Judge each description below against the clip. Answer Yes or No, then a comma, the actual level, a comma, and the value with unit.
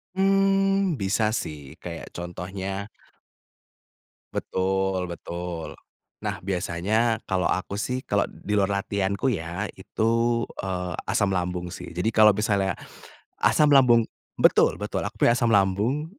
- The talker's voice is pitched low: Yes, low, 100 Hz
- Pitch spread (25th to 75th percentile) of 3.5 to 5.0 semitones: Yes, average, 4.2 semitones